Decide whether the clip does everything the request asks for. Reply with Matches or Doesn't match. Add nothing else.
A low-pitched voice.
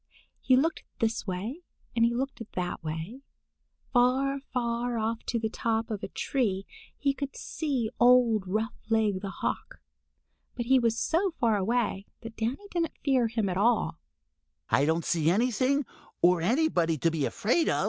Doesn't match